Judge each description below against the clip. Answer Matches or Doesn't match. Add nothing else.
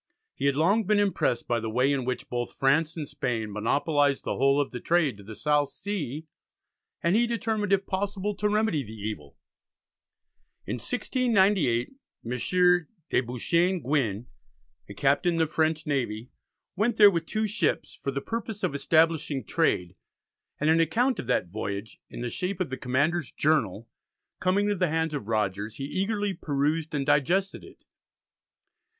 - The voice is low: Doesn't match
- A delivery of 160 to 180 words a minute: Matches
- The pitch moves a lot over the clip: Matches